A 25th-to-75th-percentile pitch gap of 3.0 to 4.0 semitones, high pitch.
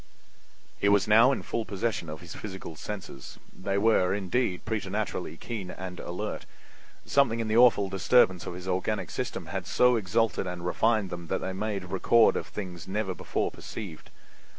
No: average, 3.5 semitones; low, 100 Hz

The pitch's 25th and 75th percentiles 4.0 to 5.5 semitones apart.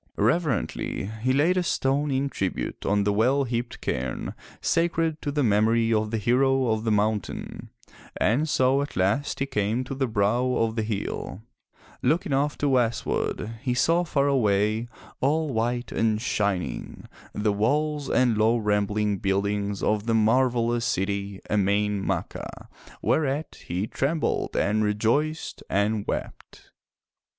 Yes: average, 4.7 semitones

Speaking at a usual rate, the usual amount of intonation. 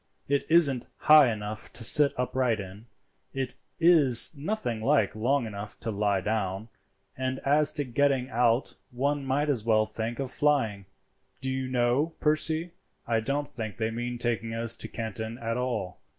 Yes: average, 165 wpm; average, 4.0 semitones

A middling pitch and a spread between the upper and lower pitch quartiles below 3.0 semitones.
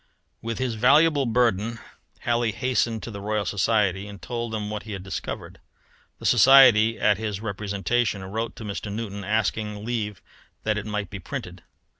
No: low, 110 Hz; narrow, 2.4 semitones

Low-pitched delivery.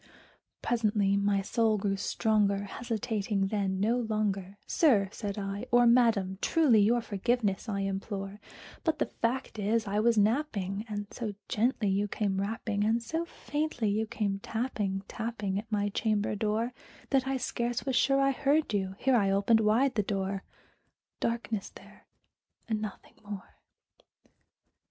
No: high, 215 Hz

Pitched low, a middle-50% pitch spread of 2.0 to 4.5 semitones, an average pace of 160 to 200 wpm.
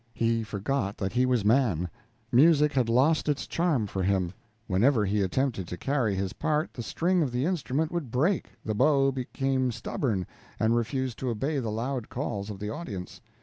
No: low, 125 Hz; average, 4.9 semitones; average, 185 wpm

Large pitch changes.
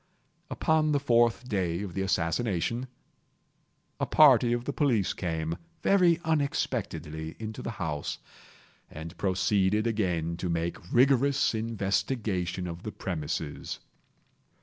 Yes: wide, 6.2 semitones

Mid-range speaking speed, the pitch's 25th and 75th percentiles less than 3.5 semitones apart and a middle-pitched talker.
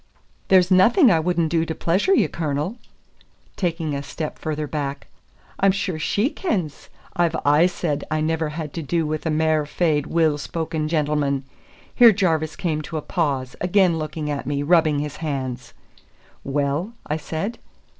Yes: average, 165 wpm; average, 2.7 semitones; medium, 160 Hz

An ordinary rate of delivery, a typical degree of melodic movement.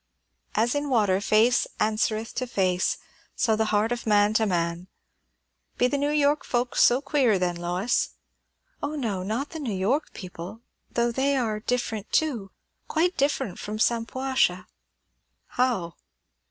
Yes: average, 150 wpm; average, 4.8 semitones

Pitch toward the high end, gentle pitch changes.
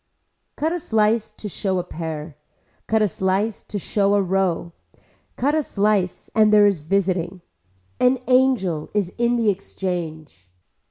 No: high, 200 Hz; average, 3.7 semitones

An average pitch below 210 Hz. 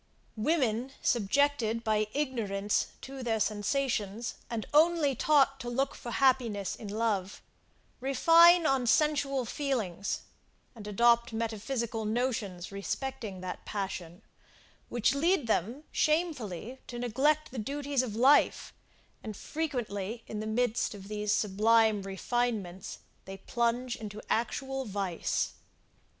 No: high, 235 Hz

